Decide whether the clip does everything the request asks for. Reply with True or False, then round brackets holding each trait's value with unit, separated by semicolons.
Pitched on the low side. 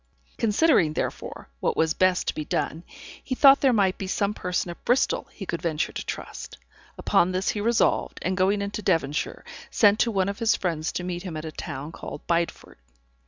False (185 Hz)